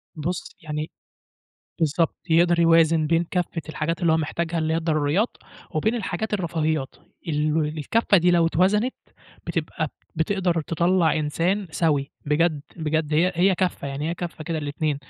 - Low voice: No, medium, 165 Hz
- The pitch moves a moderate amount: No, narrow, 2.2 semitones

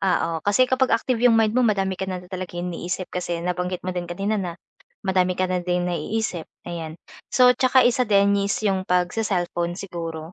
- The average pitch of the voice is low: No, medium, 185 Hz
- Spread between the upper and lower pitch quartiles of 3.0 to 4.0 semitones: Yes, average, 3.3 semitones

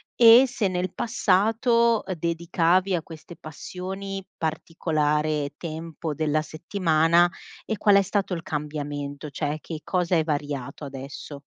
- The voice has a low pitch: No, medium, 165 Hz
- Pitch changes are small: No, average, 3.8 semitones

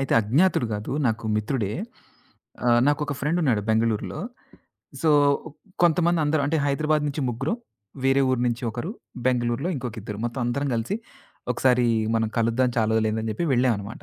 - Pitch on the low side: Yes, low, 125 Hz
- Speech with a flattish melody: No, average, 4.3 semitones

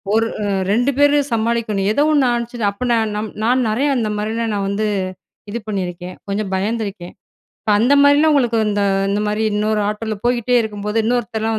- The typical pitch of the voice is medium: No, high, 220 Hz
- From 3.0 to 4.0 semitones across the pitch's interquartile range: No, narrow, 2.4 semitones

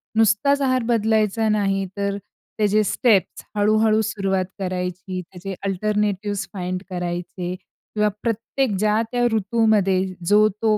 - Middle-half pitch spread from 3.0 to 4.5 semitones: No, narrow, 2.4 semitones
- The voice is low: No, high, 210 Hz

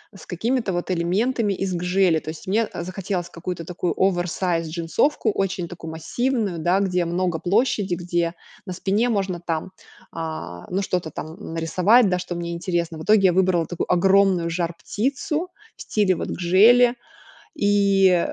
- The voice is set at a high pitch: No, medium, 180 Hz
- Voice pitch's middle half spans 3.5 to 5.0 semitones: No, average, 2.7 semitones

